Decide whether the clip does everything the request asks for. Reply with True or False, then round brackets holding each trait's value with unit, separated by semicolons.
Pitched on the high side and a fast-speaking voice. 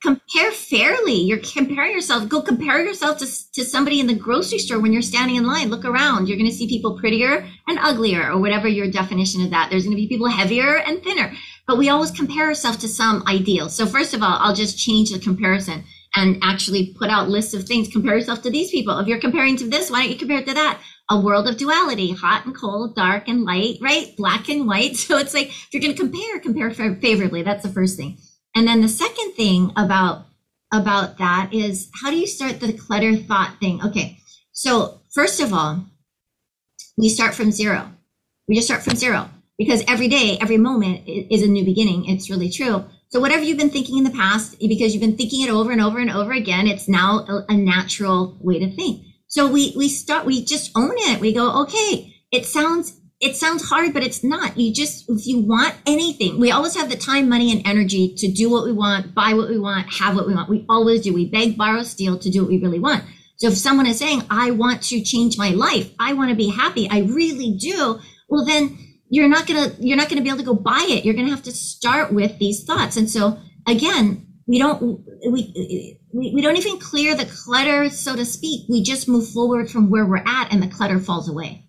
True (225 Hz; 230 wpm)